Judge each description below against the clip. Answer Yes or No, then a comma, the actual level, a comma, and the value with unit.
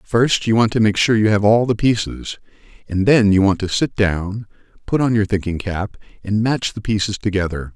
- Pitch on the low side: Yes, low, 105 Hz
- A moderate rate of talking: No, fast, 215 wpm